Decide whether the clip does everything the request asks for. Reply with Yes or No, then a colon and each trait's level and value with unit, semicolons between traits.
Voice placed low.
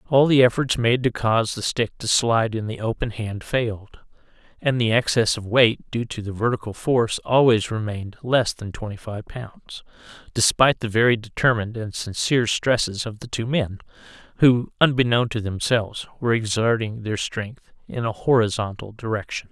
Yes: low, 115 Hz